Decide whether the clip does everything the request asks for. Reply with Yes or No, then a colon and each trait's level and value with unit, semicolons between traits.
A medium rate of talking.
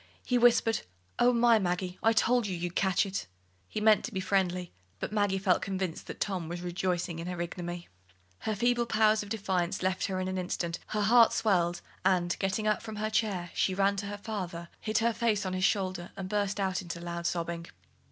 No: fast, 210 wpm